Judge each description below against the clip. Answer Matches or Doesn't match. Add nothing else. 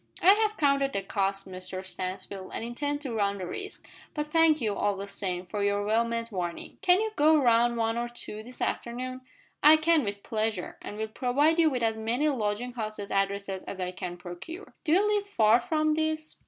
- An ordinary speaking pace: Doesn't match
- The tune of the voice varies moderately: Doesn't match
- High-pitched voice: Matches